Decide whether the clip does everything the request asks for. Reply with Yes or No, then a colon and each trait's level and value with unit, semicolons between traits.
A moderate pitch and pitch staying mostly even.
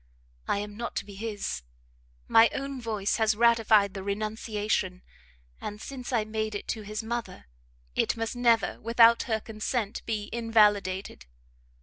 No: high, 220 Hz; narrow, 1.9 semitones